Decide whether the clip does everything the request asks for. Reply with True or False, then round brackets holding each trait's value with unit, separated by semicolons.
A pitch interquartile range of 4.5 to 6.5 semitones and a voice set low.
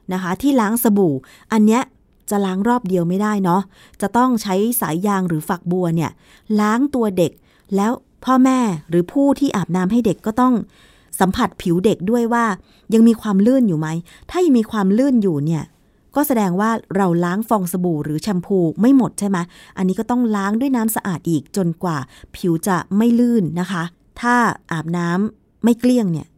False (4.9 semitones; 200 Hz)